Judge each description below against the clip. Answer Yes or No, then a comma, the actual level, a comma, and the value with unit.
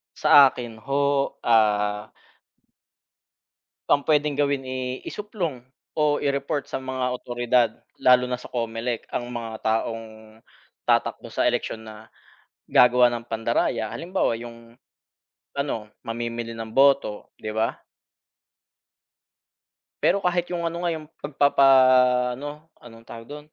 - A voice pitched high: No, low, 125 Hz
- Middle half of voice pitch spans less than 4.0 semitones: Yes, average, 3.6 semitones